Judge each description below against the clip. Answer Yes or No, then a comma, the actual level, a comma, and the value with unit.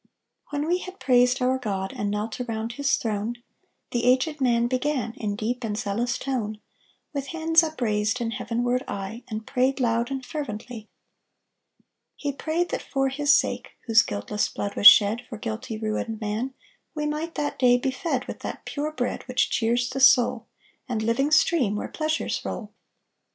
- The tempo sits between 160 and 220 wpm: Yes, average, 170 wpm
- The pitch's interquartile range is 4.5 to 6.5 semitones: No, average, 3.7 semitones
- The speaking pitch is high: Yes, high, 245 Hz